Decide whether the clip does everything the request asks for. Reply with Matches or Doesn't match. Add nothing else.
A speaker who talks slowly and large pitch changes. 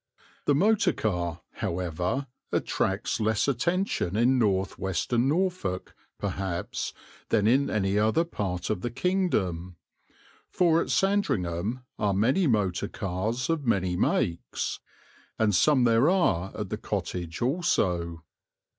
Matches